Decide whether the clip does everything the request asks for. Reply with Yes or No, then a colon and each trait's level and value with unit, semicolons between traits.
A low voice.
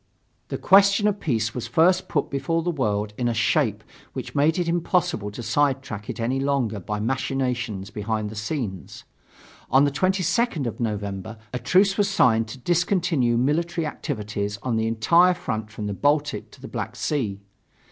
Yes: low, 130 Hz